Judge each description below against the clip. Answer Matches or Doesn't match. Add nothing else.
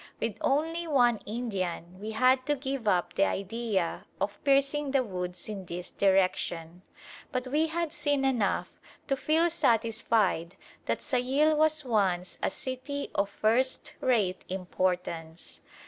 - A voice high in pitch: Matches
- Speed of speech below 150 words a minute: Matches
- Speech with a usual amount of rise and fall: Doesn't match